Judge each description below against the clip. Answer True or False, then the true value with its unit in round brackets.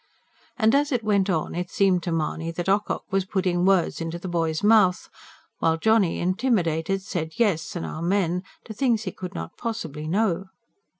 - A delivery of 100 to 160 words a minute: False (175 wpm)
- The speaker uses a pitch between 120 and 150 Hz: False (185 Hz)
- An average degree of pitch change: True (4.1 semitones)